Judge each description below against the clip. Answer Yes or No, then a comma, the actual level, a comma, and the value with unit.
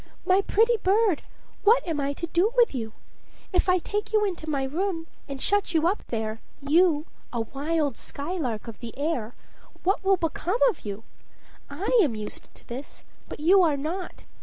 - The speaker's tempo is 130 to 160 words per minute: No, average, 180 wpm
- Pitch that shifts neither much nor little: No, wide, 6.0 semitones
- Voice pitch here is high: Yes, very high, 325 Hz